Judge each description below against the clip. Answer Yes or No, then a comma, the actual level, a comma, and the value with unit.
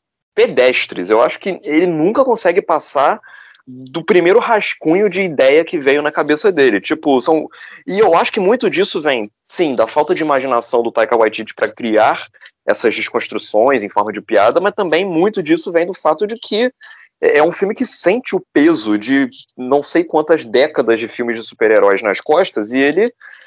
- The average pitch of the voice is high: No, medium, 165 Hz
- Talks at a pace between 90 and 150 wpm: No, fast, 185 wpm